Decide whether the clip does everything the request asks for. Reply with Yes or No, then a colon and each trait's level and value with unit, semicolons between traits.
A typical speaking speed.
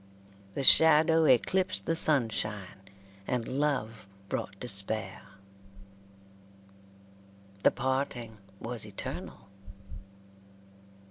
No: slow, 70 wpm